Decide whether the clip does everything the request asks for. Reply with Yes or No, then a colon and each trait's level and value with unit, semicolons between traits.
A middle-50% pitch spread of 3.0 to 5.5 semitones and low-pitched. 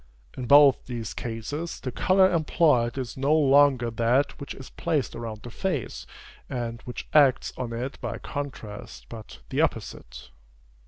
Yes: average, 3.7 semitones; low, 130 Hz